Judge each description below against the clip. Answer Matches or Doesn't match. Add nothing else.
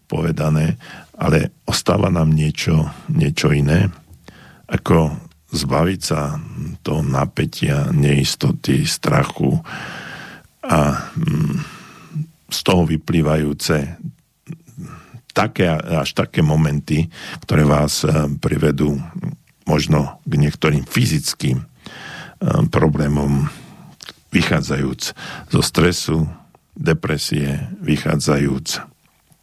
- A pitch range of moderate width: Doesn't match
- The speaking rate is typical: Doesn't match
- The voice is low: Matches